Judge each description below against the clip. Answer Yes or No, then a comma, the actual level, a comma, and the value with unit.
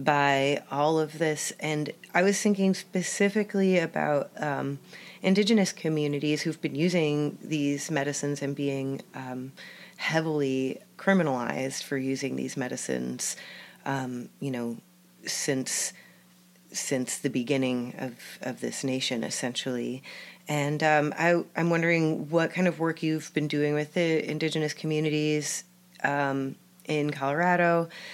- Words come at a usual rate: No, slow, 125 wpm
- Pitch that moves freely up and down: No, average, 3.7 semitones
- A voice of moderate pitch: Yes, medium, 150 Hz